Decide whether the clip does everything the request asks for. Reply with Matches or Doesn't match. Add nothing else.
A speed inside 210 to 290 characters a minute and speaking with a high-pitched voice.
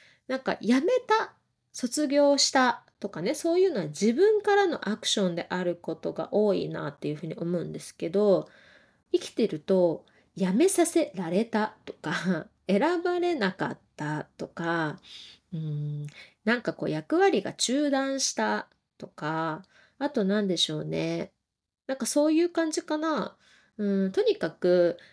Matches